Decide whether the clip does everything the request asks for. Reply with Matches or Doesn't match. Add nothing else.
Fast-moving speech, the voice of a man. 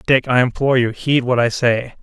Matches